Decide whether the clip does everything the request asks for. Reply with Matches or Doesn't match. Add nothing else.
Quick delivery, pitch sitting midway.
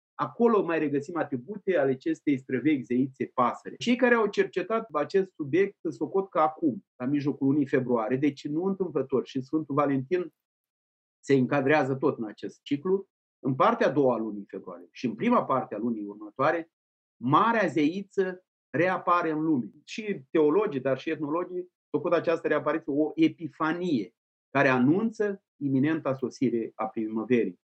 Doesn't match